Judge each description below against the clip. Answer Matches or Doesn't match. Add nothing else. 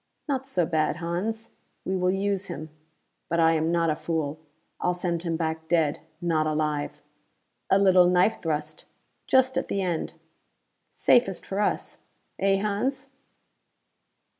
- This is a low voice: Doesn't match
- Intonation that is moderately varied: Matches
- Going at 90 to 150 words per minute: Matches